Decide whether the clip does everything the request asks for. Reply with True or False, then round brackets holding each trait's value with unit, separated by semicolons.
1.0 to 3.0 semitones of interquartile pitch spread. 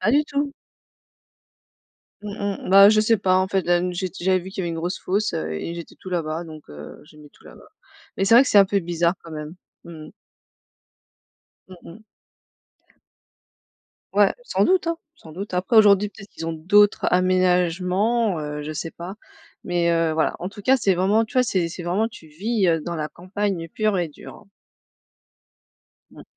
False (3.7 semitones)